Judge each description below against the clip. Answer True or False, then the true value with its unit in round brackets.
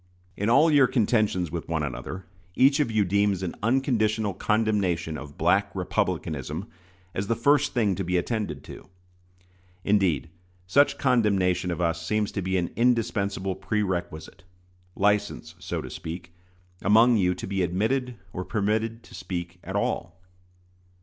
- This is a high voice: False (100 Hz)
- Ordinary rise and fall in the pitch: True (4.2 semitones)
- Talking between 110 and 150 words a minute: True (145 wpm)